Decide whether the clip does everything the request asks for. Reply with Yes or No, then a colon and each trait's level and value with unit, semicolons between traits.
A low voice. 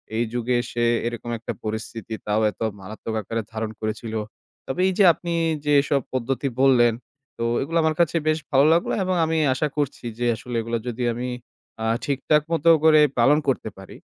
Yes: low, 125 Hz